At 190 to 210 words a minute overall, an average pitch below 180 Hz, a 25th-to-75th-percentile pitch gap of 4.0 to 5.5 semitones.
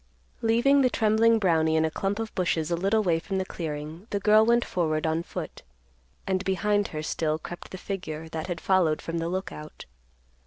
No: average, 195 wpm; medium, 185 Hz; average, 4.6 semitones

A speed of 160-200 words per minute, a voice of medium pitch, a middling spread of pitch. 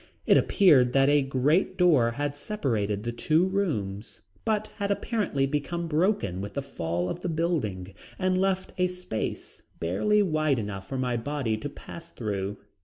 No: average, 165 wpm; medium, 145 Hz; wide, 8.6 semitones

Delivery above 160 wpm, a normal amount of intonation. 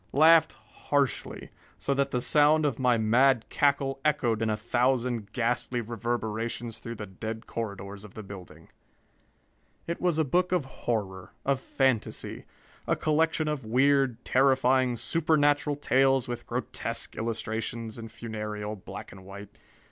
No: average, 140 wpm; average, 4.1 semitones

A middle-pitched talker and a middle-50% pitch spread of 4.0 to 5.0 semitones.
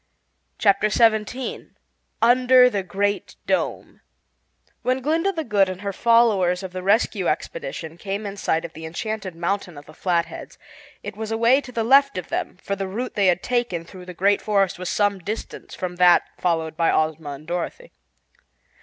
No: high, 200 Hz; average, 4.6 semitones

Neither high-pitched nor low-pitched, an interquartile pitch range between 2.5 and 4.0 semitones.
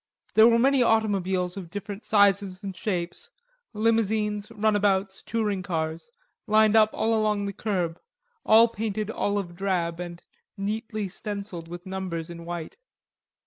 No: high, 200 Hz; average, 3.2 semitones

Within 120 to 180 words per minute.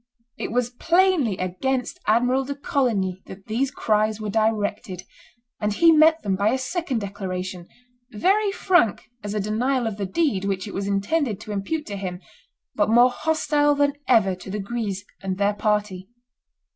Yes: average, 170 wpm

